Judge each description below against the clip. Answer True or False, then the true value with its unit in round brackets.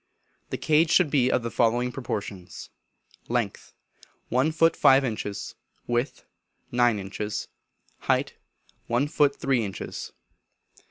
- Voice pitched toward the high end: False (125 Hz)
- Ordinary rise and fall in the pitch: True (4.1 semitones)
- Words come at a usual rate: False (115 wpm)